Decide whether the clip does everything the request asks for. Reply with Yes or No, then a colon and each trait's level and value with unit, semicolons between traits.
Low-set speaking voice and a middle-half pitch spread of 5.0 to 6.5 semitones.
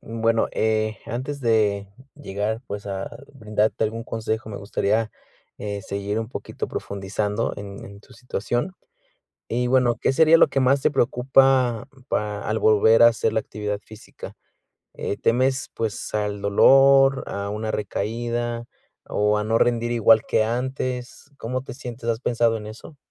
No: low, 115 Hz; average, 2.8 semitones